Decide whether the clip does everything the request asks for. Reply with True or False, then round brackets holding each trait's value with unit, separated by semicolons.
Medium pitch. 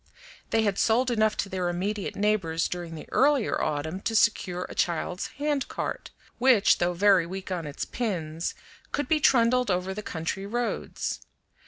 False (195 Hz)